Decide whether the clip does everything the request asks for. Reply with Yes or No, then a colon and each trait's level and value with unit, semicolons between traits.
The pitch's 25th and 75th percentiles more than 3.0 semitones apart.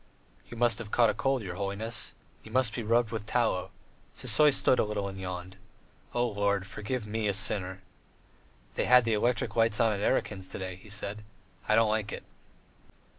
No: average, 2.7 semitones